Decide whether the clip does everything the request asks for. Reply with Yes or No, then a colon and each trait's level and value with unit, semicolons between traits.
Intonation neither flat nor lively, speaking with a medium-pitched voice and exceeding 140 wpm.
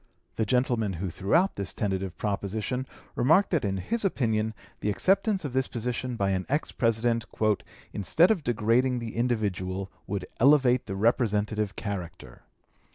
No: average, 4.3 semitones; low, 115 Hz; average, 150 wpm